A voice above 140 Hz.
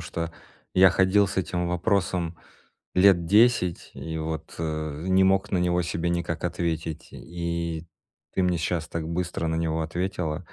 No: very low, 85 Hz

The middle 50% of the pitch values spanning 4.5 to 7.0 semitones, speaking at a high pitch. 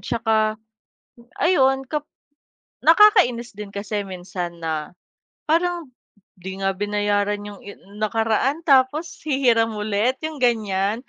Yes: average, 5.0 semitones; high, 220 Hz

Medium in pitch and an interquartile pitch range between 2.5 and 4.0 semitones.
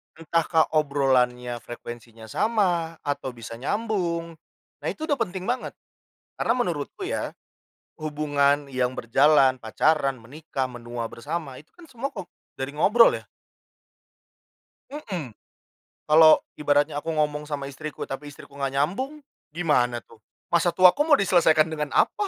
No: medium, 150 Hz; average, 4.8 semitones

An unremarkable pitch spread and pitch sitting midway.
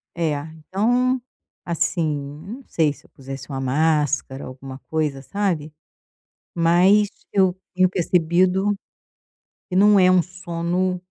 Yes: average, 3.9 semitones; medium, 170 Hz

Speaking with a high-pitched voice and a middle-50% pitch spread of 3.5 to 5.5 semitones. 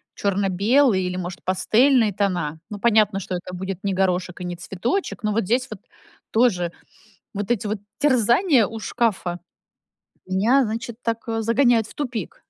Yes: high, 210 Hz; average, 4.1 semitones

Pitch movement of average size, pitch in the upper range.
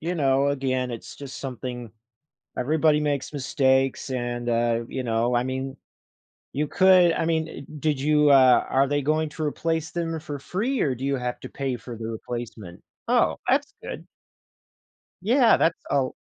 No: average, 3.8 semitones; low, 135 Hz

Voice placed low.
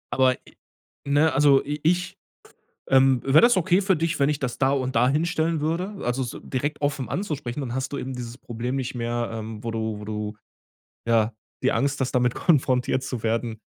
Yes: low, 130 Hz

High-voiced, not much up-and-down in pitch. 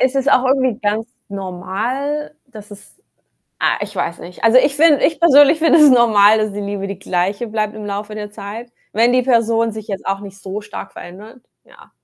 No: high, 215 Hz; average, 4.2 semitones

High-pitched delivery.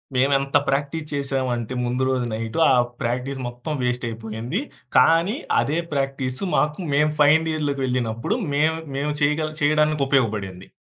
No: low, 135 Hz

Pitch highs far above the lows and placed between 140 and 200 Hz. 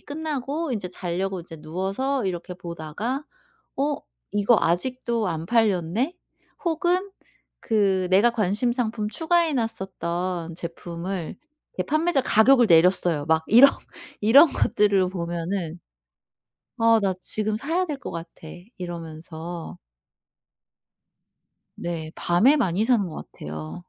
Yes: wide, 6.5 semitones; high, 195 Hz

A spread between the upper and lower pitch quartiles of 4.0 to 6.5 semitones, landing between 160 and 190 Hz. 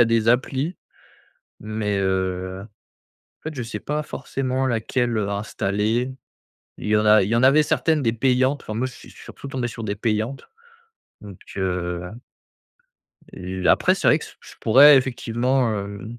No: average, 4.4 semitones; low, 115 Hz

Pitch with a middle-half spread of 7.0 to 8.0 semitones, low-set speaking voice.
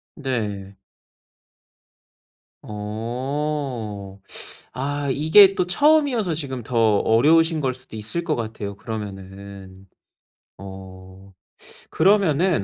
Yes: wide, 7.3 semitones; low, 120 Hz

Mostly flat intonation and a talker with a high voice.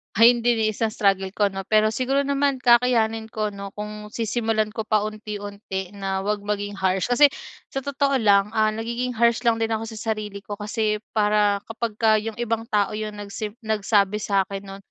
Yes: narrow, 1.9 semitones; high, 215 Hz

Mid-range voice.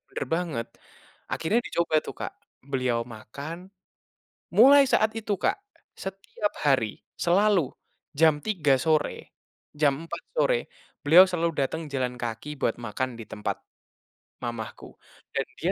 Yes: medium, 155 Hz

